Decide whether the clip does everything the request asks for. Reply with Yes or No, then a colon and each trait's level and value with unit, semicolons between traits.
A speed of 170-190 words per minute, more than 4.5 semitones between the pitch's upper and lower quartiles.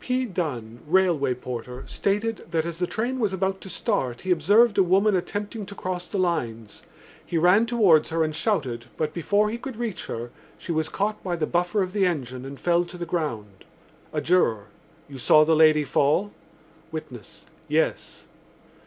Yes: average, 180 wpm; wide, 5.4 semitones